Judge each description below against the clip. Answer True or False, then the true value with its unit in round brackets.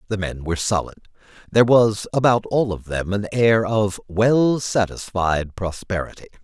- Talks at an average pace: True (150 wpm)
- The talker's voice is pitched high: False (105 Hz)